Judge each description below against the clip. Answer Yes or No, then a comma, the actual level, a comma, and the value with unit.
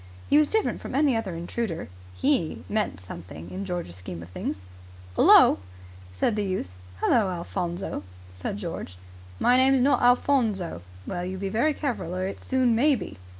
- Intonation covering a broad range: Yes, wide, 6.8 semitones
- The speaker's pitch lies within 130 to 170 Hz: No, high, 195 Hz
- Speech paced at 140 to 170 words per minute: Yes, average, 165 wpm